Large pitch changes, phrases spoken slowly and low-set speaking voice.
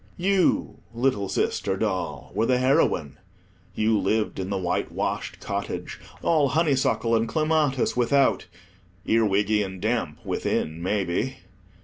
Yes: wide, 5.9 semitones; slow, 115 wpm; low, 110 Hz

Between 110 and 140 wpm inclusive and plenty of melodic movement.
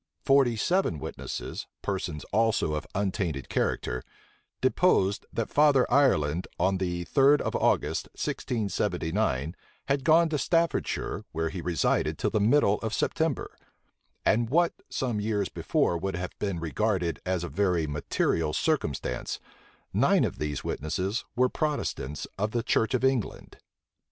Yes: slow, 135 wpm; wide, 7.2 semitones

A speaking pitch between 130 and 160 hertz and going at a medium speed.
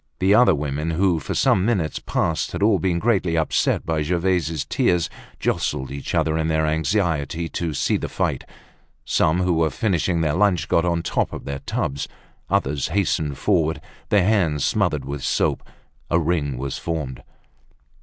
No: very low, 80 Hz; average, 170 wpm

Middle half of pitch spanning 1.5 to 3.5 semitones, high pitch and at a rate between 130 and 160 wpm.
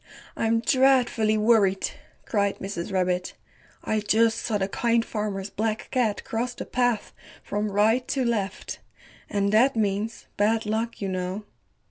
Yes: narrow, 2.4 semitones; high, 215 Hz; average, 140 wpm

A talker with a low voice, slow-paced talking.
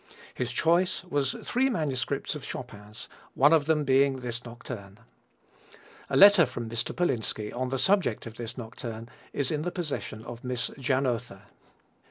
No: low, 130 Hz; average, 155 wpm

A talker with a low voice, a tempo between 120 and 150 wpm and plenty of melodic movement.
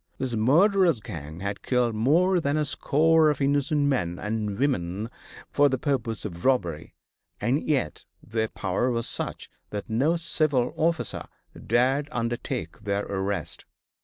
Yes: low, 125 Hz; average, 140 wpm; wide, 5.7 semitones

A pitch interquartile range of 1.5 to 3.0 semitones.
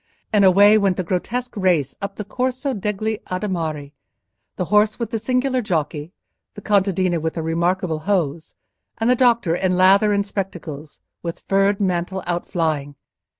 No: average, 3.9 semitones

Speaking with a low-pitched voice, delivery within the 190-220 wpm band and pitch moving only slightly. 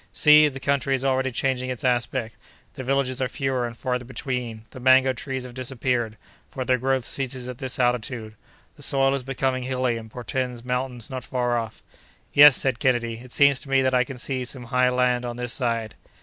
Yes: low, 125 Hz; fast, 205 wpm; narrow, 1.4 semitones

